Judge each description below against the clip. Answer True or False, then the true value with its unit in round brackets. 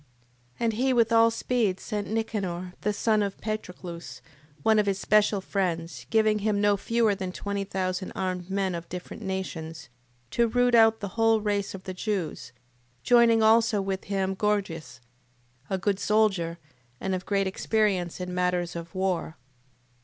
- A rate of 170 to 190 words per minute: False (160 wpm)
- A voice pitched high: True (200 Hz)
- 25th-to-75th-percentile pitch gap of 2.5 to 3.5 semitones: True (3.1 semitones)